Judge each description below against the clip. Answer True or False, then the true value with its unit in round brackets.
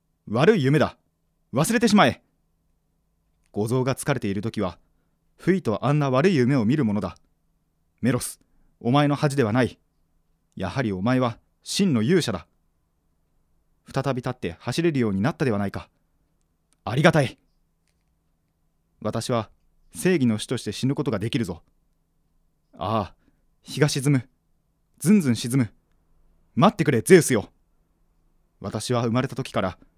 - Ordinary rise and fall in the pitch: False (8.2 semitones)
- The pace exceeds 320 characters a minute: False (260 characters per minute)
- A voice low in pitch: True (115 Hz)